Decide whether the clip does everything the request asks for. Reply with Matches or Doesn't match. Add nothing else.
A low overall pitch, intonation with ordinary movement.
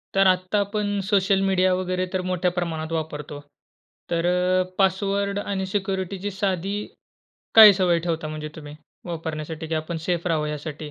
Doesn't match